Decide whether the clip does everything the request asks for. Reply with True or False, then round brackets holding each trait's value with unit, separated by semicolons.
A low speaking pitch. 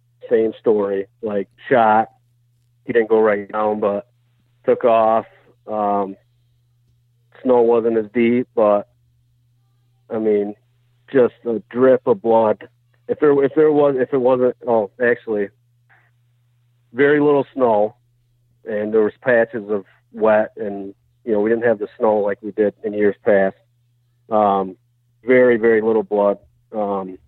True (120 Hz)